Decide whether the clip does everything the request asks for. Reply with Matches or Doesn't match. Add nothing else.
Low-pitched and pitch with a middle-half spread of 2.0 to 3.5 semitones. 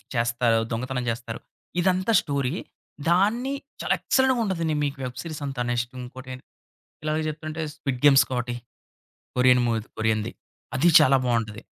Doesn't match